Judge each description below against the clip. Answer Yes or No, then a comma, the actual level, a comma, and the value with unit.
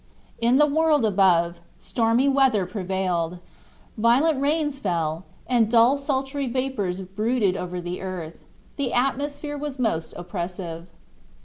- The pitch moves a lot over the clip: Yes, wide, 7.1 semitones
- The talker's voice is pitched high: Yes, high, 225 Hz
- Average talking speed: No, slow, 120 wpm